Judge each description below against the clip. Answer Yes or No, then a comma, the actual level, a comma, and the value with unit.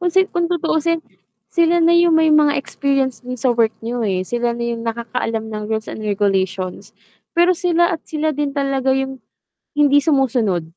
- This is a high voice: Yes, very high, 270 Hz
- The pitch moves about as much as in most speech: No, wide, 5.8 semitones